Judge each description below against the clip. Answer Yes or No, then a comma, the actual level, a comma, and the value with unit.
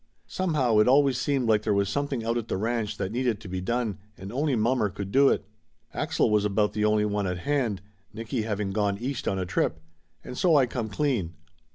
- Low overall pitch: Yes, low, 110 Hz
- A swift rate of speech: Yes, fast, 225 wpm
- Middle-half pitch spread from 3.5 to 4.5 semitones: Yes, average, 4.1 semitones